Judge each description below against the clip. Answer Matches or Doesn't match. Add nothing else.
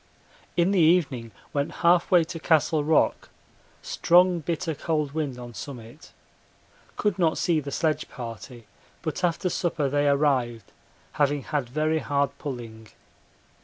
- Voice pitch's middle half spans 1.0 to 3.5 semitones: Doesn't match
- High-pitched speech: Doesn't match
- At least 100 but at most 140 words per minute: Matches